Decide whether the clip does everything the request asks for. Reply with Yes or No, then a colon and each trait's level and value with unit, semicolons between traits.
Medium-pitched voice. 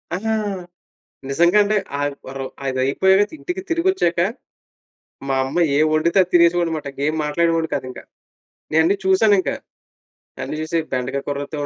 Yes: medium, 165 Hz